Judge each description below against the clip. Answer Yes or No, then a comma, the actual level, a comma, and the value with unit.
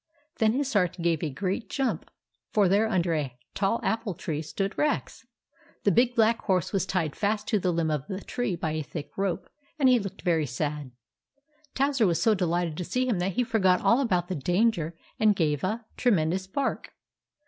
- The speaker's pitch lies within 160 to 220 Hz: Yes, high, 190 Hz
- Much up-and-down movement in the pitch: No, average, 5.0 semitones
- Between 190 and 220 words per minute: Yes, average, 195 wpm